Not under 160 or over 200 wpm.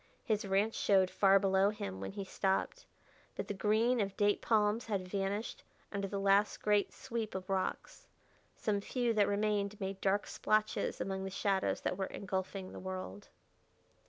Yes: average, 165 wpm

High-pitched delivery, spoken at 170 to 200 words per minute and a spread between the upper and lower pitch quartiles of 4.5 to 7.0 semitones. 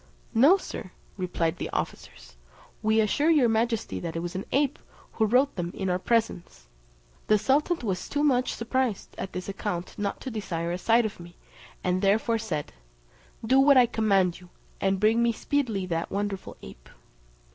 Yes: high, 215 Hz; average, 175 wpm; average, 4.9 semitones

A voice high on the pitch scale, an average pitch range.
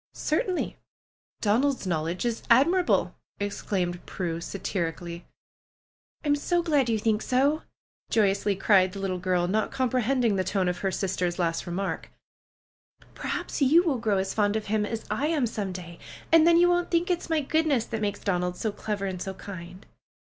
No: high, 210 Hz; wide, 6.6 semitones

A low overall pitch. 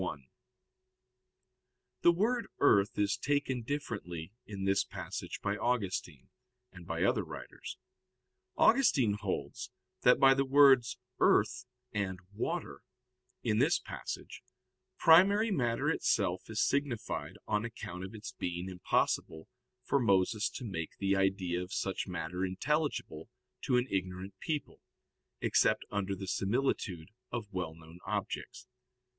Yes: low, 100 Hz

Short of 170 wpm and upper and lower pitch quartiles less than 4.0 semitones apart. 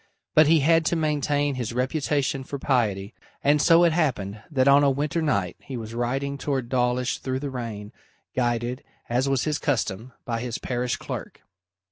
No: average, 175 wpm; average, 3.3 semitones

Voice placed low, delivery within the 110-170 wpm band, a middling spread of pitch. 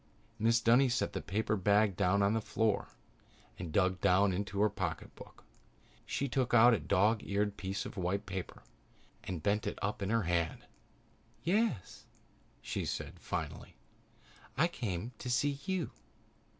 Yes: low, 105 Hz; average, 150 wpm; average, 3.6 semitones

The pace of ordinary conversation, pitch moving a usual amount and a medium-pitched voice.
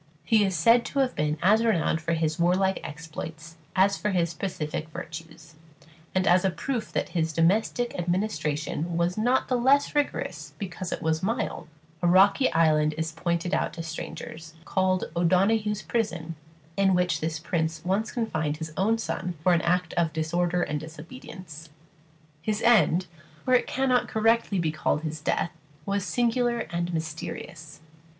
Yes: average, 160 wpm; average, 4.5 semitones; medium, 175 Hz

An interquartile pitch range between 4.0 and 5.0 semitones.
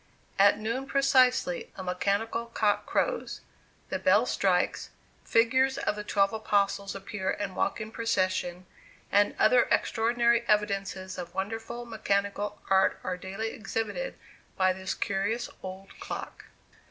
No: average, 3.0 semitones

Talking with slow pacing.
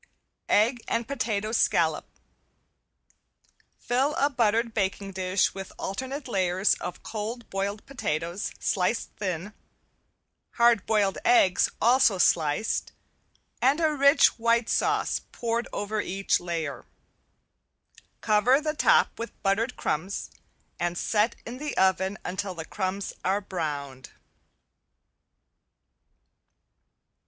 Yes: slow, 105 wpm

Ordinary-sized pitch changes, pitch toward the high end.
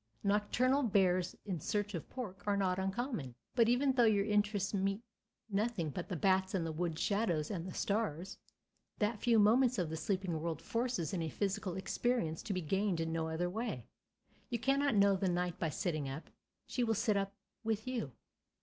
Yes: average, 4.2 semitones; high, 195 Hz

